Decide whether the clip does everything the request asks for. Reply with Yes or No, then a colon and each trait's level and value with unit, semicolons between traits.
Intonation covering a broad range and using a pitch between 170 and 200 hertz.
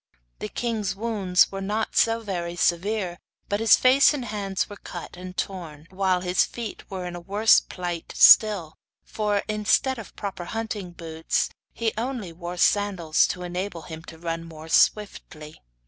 No: average, 3.6 semitones; high, 190 Hz